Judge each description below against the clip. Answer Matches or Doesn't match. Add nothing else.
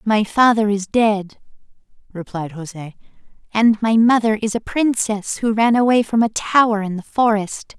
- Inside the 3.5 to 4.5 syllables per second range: Matches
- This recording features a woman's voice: Doesn't match